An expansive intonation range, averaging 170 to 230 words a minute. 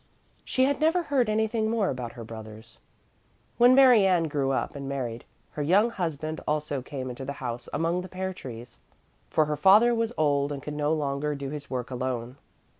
Yes: wide, 7.0 semitones; average, 190 wpm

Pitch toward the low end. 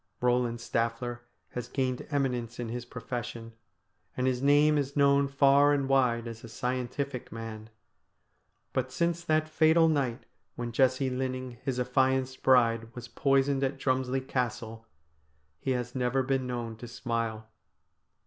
Yes: low, 125 Hz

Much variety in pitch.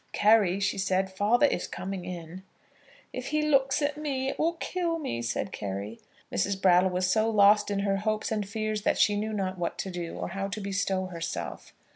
No: average, 3.2 semitones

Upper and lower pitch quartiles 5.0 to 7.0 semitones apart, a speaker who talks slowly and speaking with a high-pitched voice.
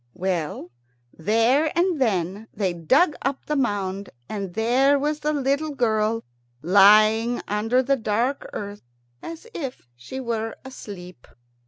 Yes: average, 5.3 semitones; slow, 130 wpm; high, 225 Hz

